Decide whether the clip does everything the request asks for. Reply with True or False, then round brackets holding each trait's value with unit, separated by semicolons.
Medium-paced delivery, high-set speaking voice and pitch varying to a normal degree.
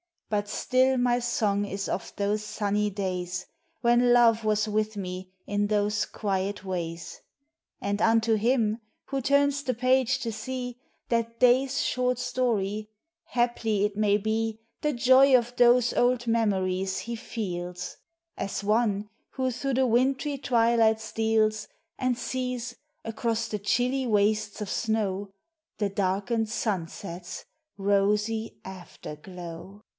False (130 wpm; 220 Hz; 3.2 semitones)